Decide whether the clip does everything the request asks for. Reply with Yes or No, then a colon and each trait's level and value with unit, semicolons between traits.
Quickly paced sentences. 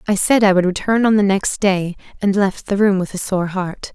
Yes: fast, 260 wpm